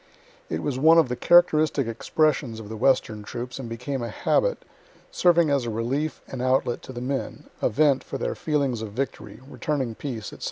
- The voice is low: Yes, low, 130 Hz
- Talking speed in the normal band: Yes, average, 195 wpm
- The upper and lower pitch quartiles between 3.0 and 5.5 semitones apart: Yes, average, 4.1 semitones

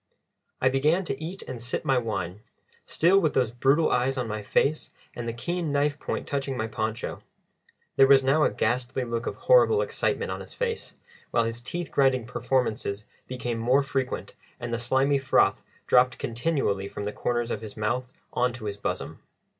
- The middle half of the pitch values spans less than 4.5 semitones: Yes, average, 3.2 semitones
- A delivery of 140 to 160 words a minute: No, average, 185 wpm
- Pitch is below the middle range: Yes, low, 125 Hz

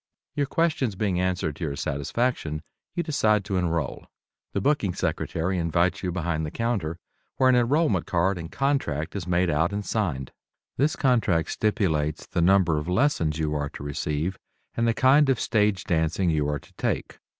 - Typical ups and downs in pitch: No, wide, 6.3 semitones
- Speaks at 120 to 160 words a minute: No, average, 175 wpm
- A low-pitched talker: Yes, very low, 90 Hz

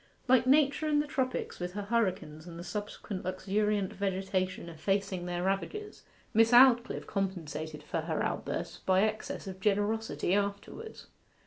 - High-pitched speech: Yes, high, 200 Hz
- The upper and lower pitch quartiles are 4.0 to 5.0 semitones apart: No, average, 3.4 semitones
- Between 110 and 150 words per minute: Yes, average, 140 wpm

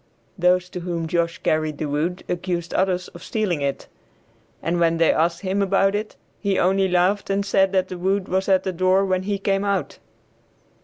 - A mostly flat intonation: Yes, narrow, 2.2 semitones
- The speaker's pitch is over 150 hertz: Yes, medium, 185 Hz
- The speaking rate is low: No, average, 195 wpm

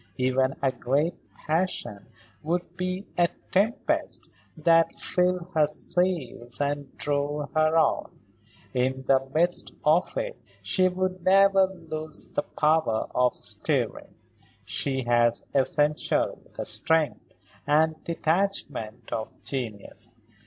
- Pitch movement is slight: No, average, 5.1 semitones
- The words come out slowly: Yes, slow, 110 wpm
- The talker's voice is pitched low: No, medium, 155 Hz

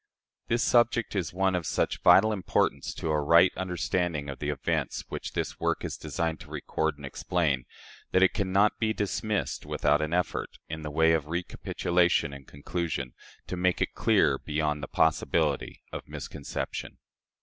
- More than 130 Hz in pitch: No, very low, 85 Hz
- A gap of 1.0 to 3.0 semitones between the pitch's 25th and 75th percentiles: No, average, 3.6 semitones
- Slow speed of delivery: No, average, 170 wpm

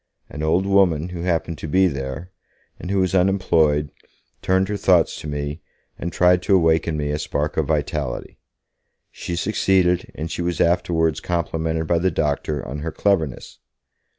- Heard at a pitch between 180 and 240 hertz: No, very low, 85 Hz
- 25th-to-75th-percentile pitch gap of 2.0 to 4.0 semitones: Yes, average, 3.1 semitones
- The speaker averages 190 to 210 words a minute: No, average, 170 wpm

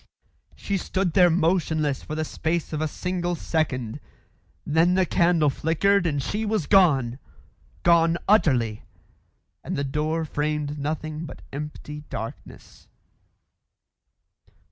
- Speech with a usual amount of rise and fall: Yes, average, 3.0 semitones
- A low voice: No, medium, 160 Hz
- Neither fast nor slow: No, slow, 120 wpm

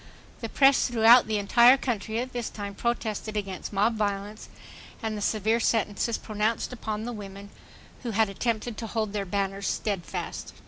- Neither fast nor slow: Yes, average, 165 wpm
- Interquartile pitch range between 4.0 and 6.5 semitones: No, narrow, 2.5 semitones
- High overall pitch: Yes, high, 215 Hz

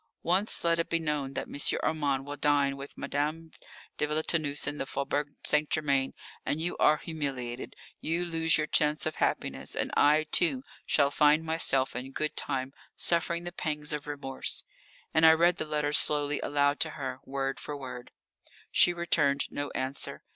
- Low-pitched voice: No, medium, 150 Hz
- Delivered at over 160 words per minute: Yes, average, 175 wpm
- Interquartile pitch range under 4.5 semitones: Yes, narrow, 2.4 semitones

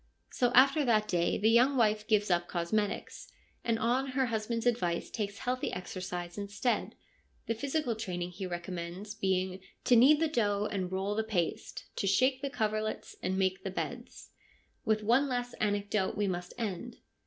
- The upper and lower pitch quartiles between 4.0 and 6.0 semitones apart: Yes, average, 4.3 semitones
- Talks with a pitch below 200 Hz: No, high, 215 Hz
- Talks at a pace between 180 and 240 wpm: No, average, 170 wpm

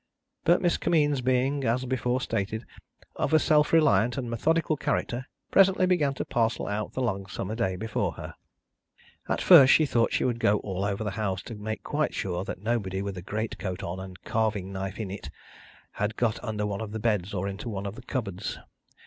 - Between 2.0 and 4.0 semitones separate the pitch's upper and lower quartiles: No, average, 4.6 semitones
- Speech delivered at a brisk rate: Yes, fast, 210 wpm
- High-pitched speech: No, low, 110 Hz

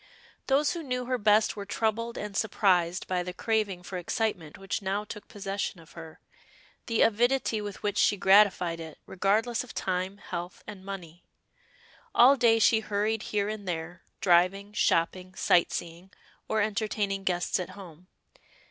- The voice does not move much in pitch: No, average, 3.3 semitones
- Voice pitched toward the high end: Yes, high, 200 Hz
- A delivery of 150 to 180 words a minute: Yes, average, 155 wpm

